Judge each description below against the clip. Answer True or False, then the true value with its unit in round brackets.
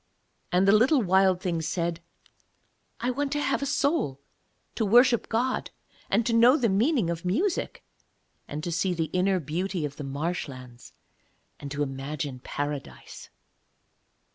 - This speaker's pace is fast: False (145 wpm)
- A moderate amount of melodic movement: False (8.0 semitones)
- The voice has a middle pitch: True (180 Hz)